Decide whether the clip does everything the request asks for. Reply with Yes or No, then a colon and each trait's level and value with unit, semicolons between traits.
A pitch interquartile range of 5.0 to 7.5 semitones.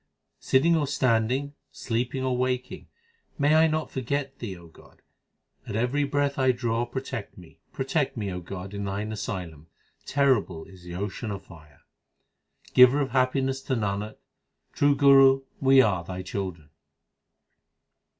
Yes: wide, 5.5 semitones